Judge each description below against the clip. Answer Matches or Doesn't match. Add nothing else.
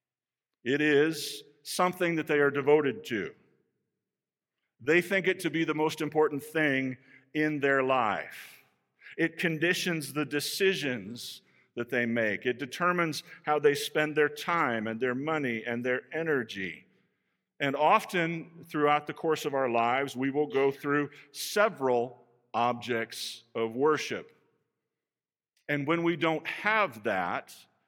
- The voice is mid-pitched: Matches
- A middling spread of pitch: Matches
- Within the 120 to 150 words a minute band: Matches